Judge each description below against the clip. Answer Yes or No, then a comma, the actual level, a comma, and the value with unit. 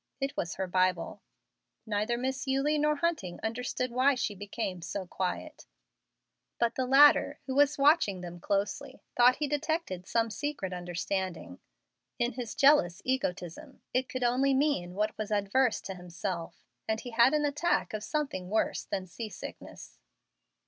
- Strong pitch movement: Yes, wide, 6.5 semitones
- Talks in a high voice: Yes, high, 235 Hz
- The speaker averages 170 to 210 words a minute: No, average, 155 wpm